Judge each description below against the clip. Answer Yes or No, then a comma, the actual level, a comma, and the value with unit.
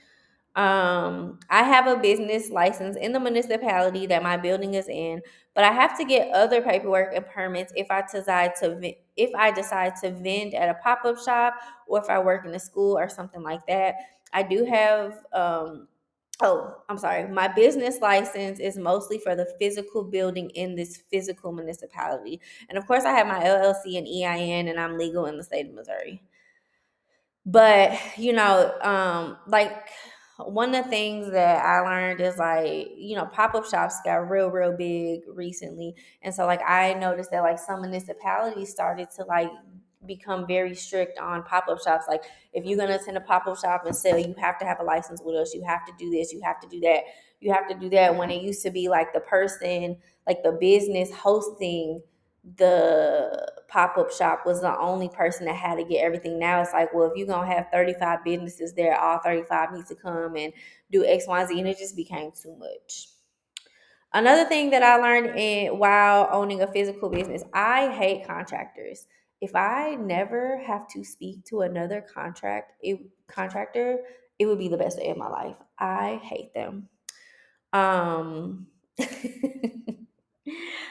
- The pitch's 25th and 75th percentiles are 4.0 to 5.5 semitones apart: No, average, 3.2 semitones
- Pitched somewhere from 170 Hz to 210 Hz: Yes, high, 190 Hz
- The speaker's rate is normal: Yes, average, 185 wpm